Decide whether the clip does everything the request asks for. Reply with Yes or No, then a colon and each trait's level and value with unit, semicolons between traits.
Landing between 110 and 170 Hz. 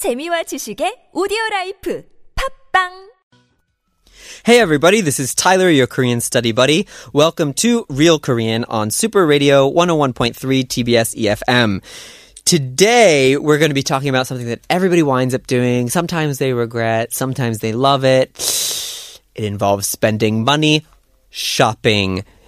Yes: medium, 140 Hz